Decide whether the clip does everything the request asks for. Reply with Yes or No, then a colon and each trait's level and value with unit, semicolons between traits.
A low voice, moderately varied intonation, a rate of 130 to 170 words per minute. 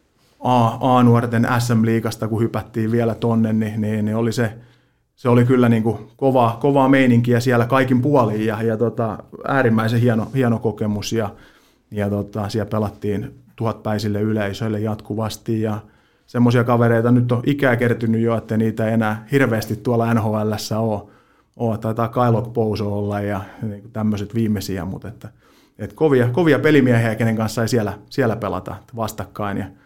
No: low, 115 Hz; narrow, 2.1 semitones; fast, 155 wpm